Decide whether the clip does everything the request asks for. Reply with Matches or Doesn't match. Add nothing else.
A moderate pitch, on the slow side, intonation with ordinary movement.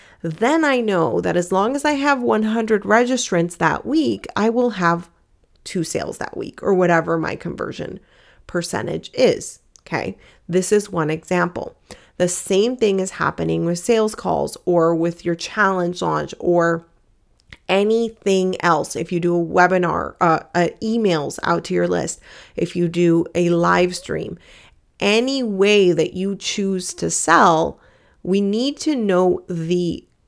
Doesn't match